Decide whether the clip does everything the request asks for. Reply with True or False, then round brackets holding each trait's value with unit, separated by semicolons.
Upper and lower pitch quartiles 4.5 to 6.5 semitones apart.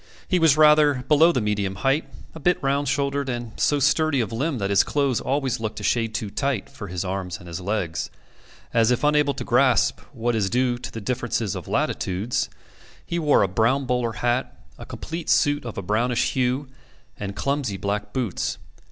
True (5.1 semitones)